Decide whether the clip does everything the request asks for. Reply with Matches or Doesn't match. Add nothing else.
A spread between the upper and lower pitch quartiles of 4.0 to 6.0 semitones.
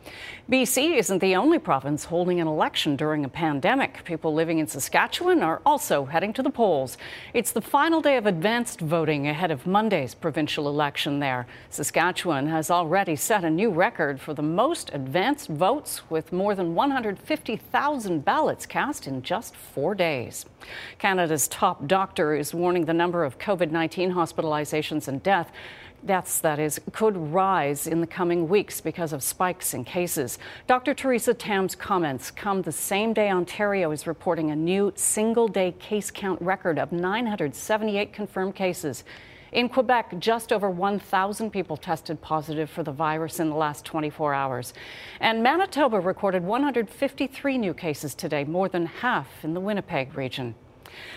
Matches